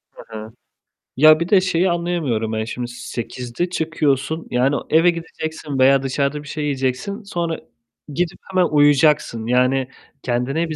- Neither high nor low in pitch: Yes, medium, 145 Hz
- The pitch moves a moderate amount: Yes, average, 4.5 semitones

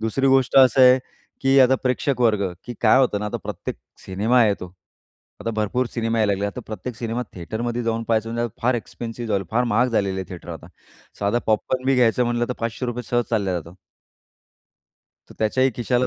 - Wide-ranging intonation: No, average, 2.8 semitones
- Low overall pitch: Yes, low, 115 Hz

